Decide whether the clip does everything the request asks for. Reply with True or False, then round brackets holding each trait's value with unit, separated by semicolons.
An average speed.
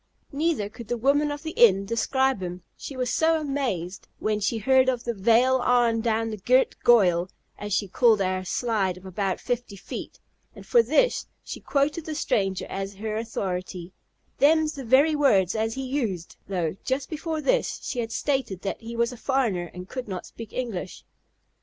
True (185 wpm)